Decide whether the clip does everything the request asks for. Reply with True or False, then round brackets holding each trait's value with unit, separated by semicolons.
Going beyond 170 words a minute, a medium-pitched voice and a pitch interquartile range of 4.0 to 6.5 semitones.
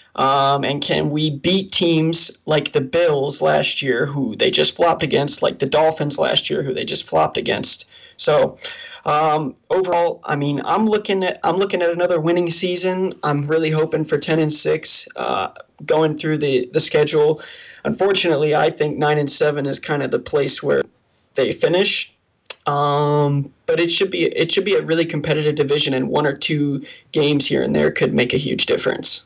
True (190 wpm; 155 Hz; 4.3 semitones)